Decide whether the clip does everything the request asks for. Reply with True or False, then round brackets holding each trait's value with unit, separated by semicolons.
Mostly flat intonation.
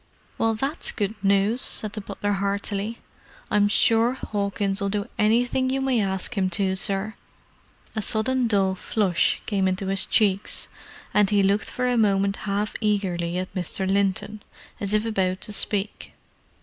True (2.0 semitones)